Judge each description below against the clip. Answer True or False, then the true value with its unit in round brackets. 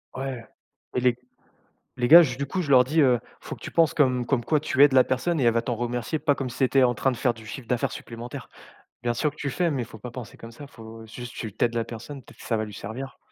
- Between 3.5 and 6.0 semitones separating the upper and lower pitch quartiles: False (2.9 semitones)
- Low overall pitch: True (125 Hz)